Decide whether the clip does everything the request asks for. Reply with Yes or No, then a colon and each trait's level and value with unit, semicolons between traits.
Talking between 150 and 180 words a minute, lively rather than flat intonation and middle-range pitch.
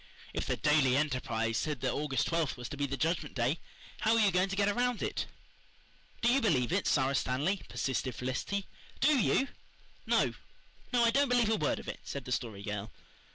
No: average, 200 wpm; wide, 8.0 semitones; medium, 150 Hz